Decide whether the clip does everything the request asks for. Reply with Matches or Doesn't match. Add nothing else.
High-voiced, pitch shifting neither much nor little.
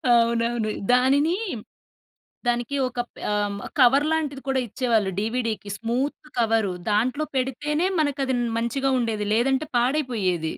Matches